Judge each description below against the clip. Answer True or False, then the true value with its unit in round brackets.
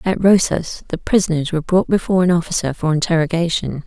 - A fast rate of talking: False (170 wpm)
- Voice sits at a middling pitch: True (170 Hz)